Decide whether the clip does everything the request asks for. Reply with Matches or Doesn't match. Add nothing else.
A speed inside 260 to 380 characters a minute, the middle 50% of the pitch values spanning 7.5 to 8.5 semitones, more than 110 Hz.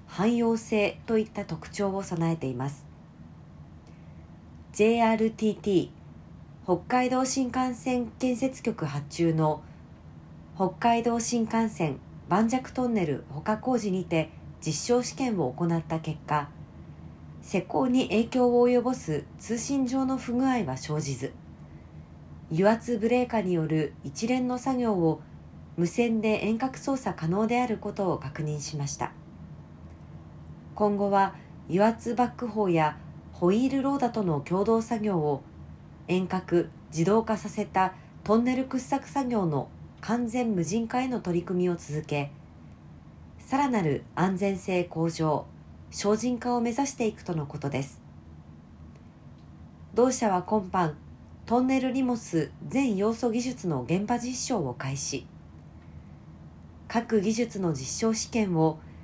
Doesn't match